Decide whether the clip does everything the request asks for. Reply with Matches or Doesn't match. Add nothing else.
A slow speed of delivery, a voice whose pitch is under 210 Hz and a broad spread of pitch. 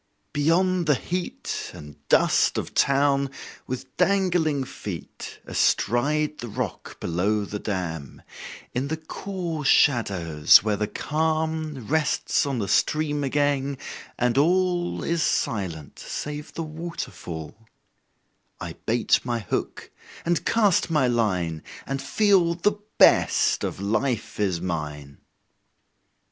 Matches